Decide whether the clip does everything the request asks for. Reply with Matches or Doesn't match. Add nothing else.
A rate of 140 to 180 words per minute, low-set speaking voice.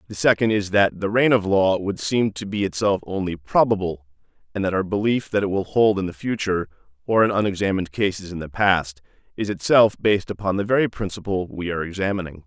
Doesn't match